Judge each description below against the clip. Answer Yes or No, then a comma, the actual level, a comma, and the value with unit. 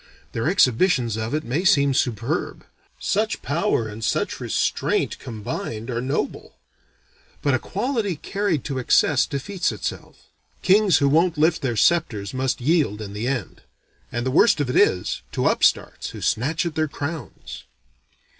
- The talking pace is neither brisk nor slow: Yes, average, 155 wpm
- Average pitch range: No, wide, 5.9 semitones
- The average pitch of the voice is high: No, medium, 140 Hz